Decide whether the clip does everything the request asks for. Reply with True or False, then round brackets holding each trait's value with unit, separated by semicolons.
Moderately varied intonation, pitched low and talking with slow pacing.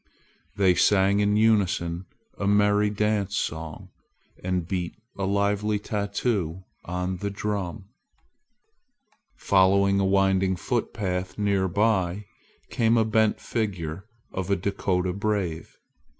False (2.0 semitones; 100 Hz; 110 wpm)